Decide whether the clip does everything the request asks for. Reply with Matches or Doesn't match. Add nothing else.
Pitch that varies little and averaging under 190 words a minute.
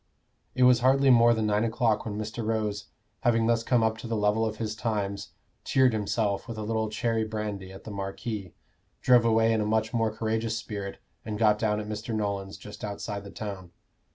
Doesn't match